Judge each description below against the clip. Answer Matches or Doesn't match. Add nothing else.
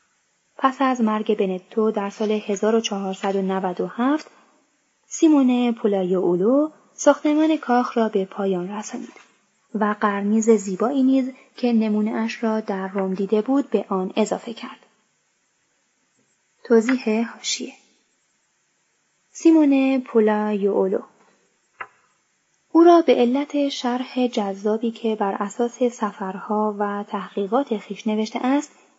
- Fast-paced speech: Doesn't match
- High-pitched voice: Matches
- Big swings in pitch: Doesn't match